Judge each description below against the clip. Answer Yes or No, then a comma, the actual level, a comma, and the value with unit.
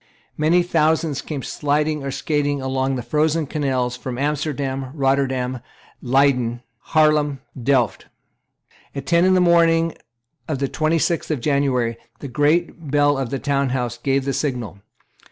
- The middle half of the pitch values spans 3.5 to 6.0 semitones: No, average, 2.7 semitones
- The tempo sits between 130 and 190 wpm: Yes, average, 145 wpm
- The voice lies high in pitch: No, medium, 140 Hz